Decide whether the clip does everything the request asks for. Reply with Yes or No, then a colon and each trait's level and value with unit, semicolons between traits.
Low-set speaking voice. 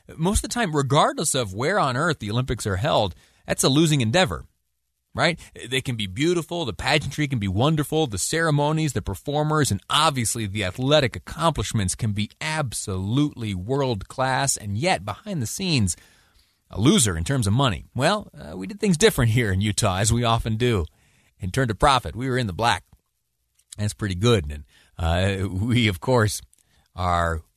Yes: low, 115 Hz